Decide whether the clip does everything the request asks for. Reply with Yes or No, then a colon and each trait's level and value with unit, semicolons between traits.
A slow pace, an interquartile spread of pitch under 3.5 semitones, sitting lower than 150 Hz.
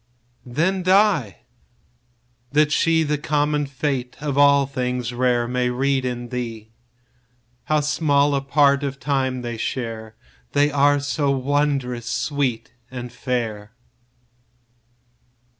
Yes: slow, 115 wpm; average, 2.9 semitones; low, 135 Hz